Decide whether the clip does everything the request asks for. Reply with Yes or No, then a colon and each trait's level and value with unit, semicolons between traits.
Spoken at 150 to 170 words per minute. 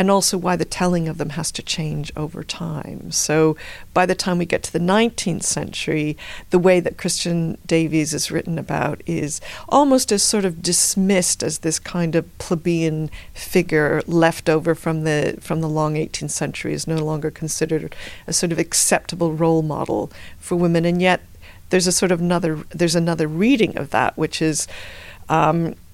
No: average, 180 wpm